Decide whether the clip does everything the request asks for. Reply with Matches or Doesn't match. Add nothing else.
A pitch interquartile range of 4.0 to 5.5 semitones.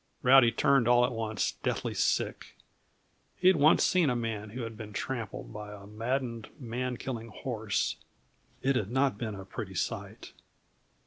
Doesn't match